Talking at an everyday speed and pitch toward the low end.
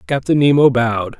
Yes: average, 150 wpm; low, 130 Hz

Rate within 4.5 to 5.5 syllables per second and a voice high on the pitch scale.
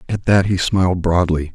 No: 5.1 syllables/s; very low, 90 Hz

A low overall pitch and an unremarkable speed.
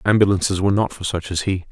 No: very low, 95 Hz; fast, 245 wpm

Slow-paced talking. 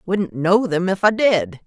No: fast, 215 wpm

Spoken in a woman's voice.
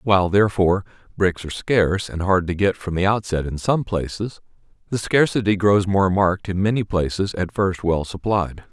No: male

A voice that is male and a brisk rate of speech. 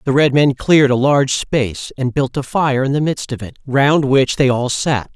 Yes: male; fast, 245 wpm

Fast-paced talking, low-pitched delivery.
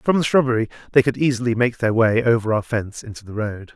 Yes: fast, 240 wpm; low, 120 Hz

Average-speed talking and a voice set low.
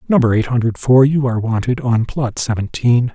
Yes: average, 190 wpm; low, 120 Hz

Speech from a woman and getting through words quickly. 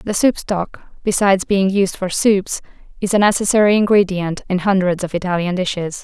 No: female; average, 170 wpm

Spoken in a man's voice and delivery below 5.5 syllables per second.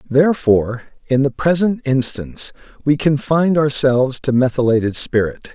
Yes: male; 5.1 syllables/s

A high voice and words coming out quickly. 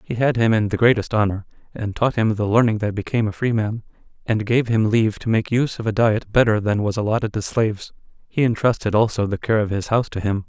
No: low, 110 Hz; fast, 245 wpm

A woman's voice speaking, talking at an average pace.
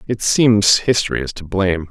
No: male; average, 190 wpm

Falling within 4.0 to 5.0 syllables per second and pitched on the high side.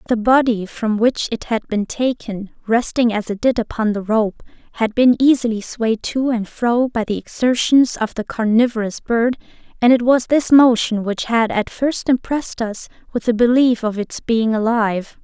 Yes: 4.6 syllables/s; high, 230 Hz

